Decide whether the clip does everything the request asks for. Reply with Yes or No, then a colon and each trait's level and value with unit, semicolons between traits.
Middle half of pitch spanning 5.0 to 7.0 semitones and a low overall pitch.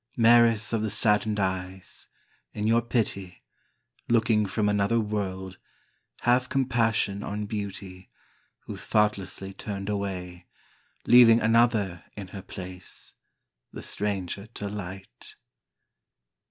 No: average, 2.8 semitones; low, 105 Hz